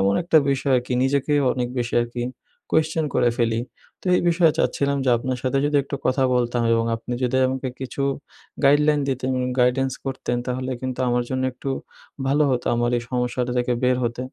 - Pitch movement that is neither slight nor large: No, narrow, 2.0 semitones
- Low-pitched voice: Yes, low, 130 Hz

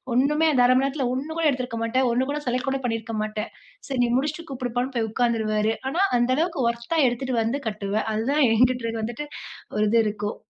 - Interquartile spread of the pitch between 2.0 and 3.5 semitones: Yes, average, 3.1 semitones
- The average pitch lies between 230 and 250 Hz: Yes, high, 245 Hz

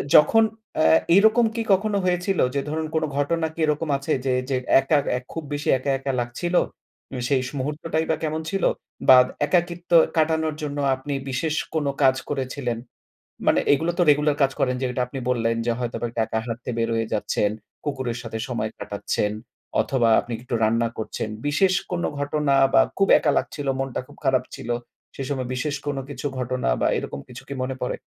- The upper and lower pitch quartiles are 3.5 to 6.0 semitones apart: Yes, average, 4.0 semitones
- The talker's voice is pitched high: No, medium, 140 Hz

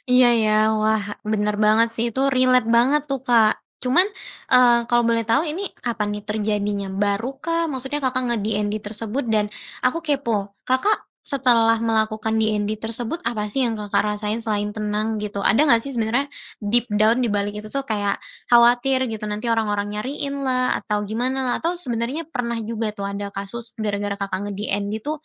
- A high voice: Yes, high, 225 Hz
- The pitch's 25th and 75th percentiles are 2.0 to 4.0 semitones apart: Yes, average, 3.2 semitones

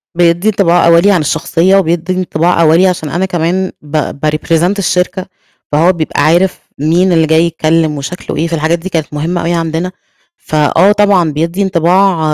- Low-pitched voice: No, medium, 170 Hz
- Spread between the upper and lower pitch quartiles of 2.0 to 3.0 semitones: Yes, narrow, 2.4 semitones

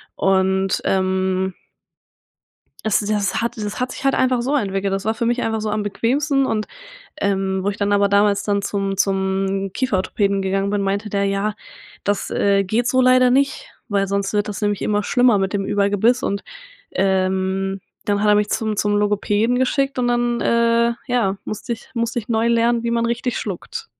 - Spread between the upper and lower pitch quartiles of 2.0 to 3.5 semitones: Yes, average, 3.1 semitones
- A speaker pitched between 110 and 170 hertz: No, high, 205 Hz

